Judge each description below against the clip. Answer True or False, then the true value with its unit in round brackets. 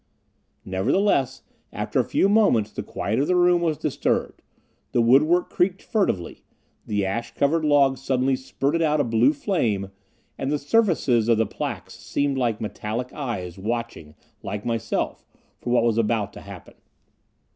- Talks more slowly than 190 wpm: True (155 wpm)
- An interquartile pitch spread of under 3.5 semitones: False (5.3 semitones)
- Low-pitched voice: True (130 Hz)